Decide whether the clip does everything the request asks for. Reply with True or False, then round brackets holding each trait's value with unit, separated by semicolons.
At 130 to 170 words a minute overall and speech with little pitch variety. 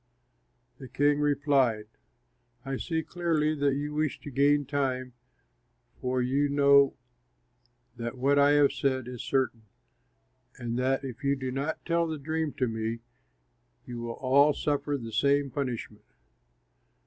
True (140 wpm; 2.3 semitones)